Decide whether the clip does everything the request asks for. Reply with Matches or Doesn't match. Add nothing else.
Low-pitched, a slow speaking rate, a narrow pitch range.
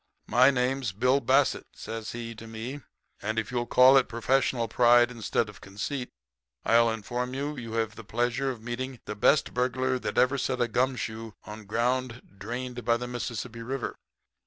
Doesn't match